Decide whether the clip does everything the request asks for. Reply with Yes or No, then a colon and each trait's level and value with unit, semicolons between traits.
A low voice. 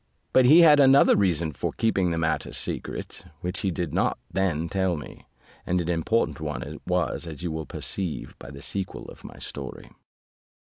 Yes: very low, 85 Hz